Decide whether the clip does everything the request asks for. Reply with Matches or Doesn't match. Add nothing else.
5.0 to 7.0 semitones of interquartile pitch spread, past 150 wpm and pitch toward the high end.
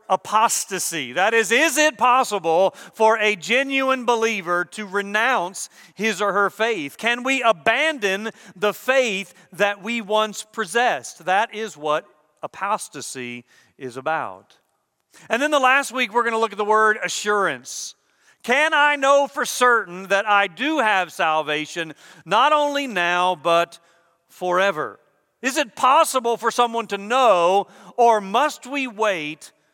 Doesn't match